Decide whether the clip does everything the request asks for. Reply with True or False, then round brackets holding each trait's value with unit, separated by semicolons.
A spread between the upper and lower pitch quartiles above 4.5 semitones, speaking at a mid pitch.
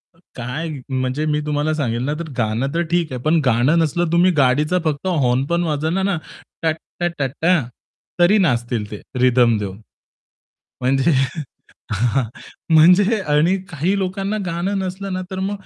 True (5.5 semitones; 155 Hz)